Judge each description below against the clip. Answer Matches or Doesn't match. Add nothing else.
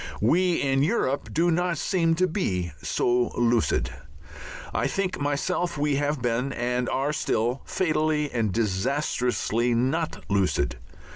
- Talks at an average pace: Doesn't match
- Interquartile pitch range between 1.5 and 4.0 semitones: Doesn't match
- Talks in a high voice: Doesn't match